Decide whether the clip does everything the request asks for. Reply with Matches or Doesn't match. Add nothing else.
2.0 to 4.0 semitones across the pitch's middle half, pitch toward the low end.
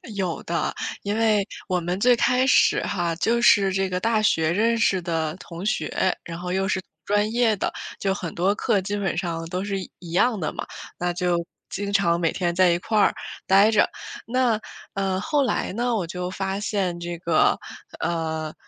Doesn't match